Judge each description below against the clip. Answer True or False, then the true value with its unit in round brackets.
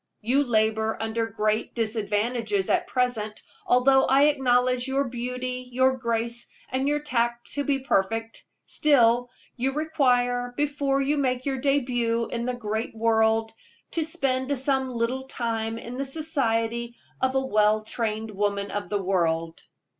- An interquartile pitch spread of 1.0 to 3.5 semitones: True (3.0 semitones)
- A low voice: False (245 Hz)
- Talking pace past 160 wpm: False (145 wpm)